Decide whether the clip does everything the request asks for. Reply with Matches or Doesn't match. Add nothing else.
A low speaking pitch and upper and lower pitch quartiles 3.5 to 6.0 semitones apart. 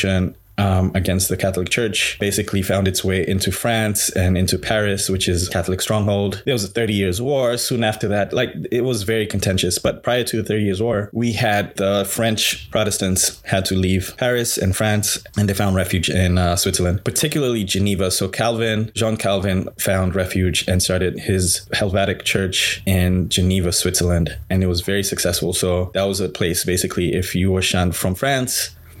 Doesn't match